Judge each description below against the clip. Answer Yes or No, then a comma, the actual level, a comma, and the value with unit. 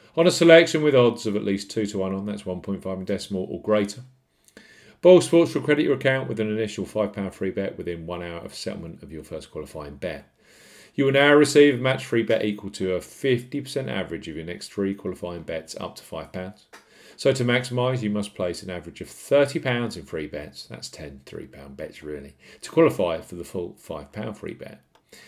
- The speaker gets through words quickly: Yes, fast, 220 wpm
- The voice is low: Yes, low, 105 Hz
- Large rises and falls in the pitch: Yes, wide, 6.1 semitones